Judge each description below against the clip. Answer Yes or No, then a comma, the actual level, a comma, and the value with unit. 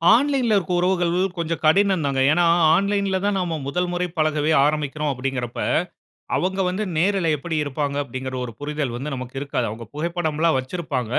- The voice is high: No, medium, 155 Hz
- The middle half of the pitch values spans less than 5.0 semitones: Yes, average, 4.6 semitones